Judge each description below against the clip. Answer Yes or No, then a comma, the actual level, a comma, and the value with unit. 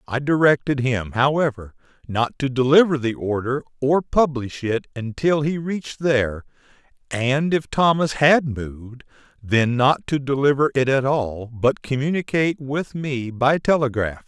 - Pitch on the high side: No, low, 135 Hz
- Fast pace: No, average, 145 wpm